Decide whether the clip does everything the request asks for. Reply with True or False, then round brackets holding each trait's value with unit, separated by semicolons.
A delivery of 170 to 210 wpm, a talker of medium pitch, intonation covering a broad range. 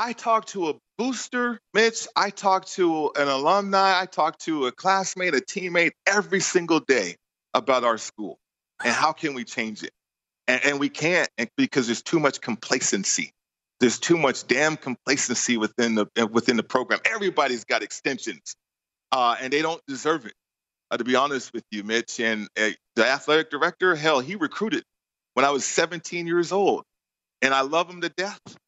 True (180 wpm; 160 Hz; 6.5 semitones)